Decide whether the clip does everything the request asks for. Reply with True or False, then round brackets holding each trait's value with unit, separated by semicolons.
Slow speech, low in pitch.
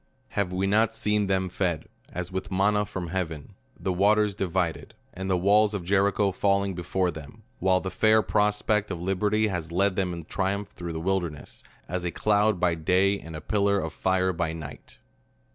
False (195 wpm; 95 Hz)